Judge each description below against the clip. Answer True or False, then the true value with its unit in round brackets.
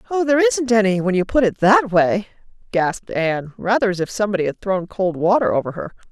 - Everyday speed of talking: False (215 wpm)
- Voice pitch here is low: False (200 Hz)